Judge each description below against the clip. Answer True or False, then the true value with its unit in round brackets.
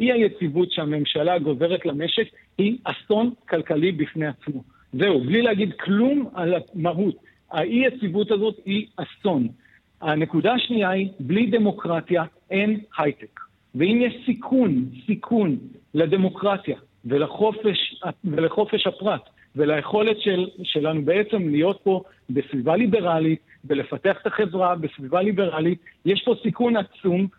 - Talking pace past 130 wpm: False (115 wpm)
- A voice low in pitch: False (185 Hz)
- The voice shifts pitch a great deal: False (4.9 semitones)